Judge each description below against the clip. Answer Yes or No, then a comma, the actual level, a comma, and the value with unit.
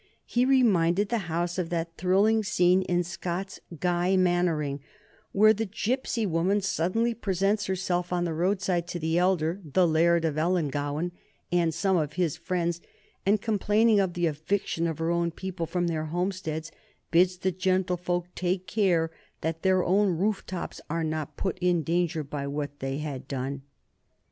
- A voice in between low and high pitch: Yes, medium, 175 Hz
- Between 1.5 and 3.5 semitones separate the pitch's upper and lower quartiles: Yes, narrow, 2.6 semitones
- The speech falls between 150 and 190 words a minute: Yes, average, 165 wpm